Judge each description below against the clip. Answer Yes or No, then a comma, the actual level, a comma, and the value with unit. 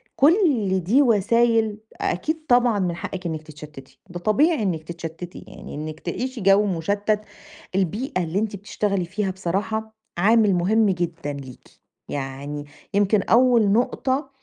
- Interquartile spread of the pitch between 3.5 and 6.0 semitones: Yes, average, 4.7 semitones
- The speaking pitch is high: Yes, high, 200 Hz